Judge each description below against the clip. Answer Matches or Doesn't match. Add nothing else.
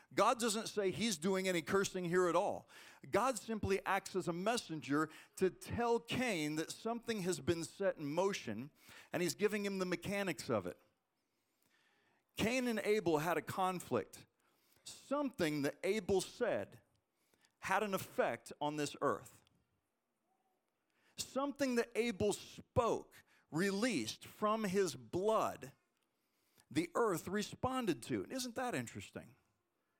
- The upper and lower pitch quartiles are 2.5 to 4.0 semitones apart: Doesn't match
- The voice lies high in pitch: Matches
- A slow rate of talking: Matches